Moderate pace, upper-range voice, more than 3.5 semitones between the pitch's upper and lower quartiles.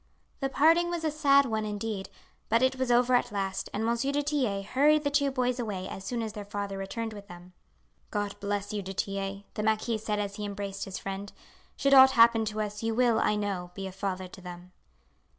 No: fast, 220 wpm; high, 215 Hz; average, 4.2 semitones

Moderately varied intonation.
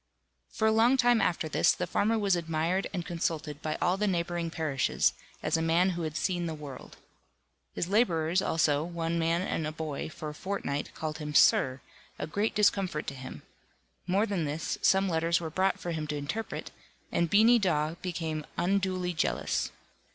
Yes: average, 3.6 semitones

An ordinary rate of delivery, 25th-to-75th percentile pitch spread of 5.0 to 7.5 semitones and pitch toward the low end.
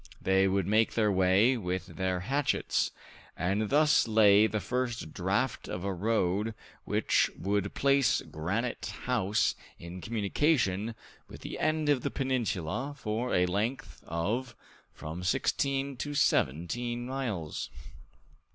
No: slow, 125 wpm; average, 5.3 semitones; low, 110 Hz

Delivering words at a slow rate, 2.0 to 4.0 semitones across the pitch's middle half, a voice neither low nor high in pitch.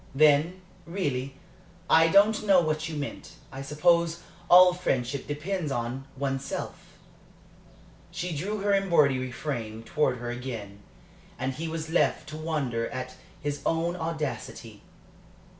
No: slow, 130 wpm; average, 4.4 semitones; medium, 150 Hz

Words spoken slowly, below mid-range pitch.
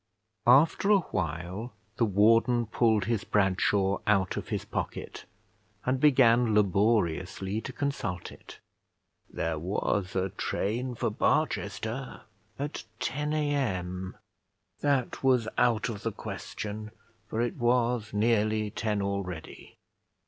Yes: slow, 115 wpm; low, 110 Hz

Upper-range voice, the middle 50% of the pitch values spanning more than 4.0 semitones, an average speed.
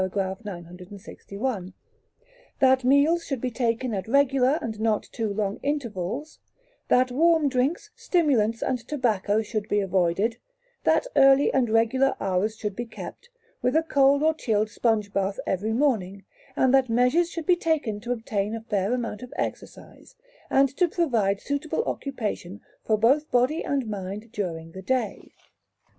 Yes: high, 235 Hz; average, 4.9 semitones; average, 150 wpm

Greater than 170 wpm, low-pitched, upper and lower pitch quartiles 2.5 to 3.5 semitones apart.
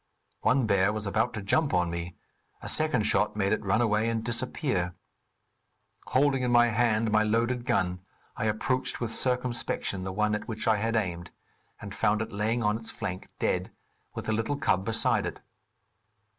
Yes: average, 180 wpm; low, 110 Hz; average, 3.0 semitones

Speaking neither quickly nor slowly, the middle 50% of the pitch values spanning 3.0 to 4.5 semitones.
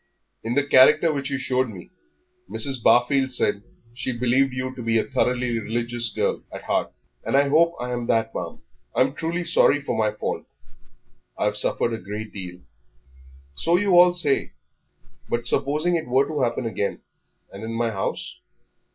Yes: average, 175 wpm; average, 3.7 semitones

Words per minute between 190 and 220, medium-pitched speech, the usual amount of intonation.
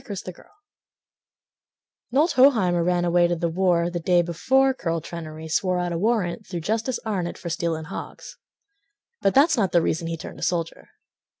No: average, 175 wpm; medium, 175 Hz; average, 3.9 semitones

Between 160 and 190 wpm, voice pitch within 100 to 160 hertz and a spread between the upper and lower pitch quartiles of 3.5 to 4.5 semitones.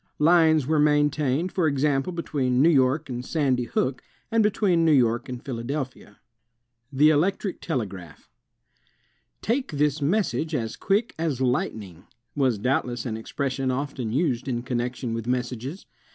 No: average, 150 wpm; low, 135 Hz; average, 4.1 semitones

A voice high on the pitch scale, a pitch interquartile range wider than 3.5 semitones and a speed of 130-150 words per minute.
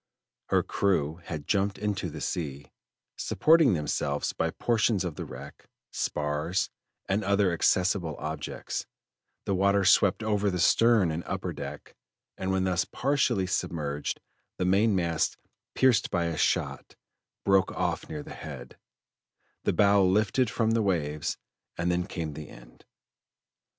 No: very low, 95 Hz; average, 4.5 semitones; average, 140 wpm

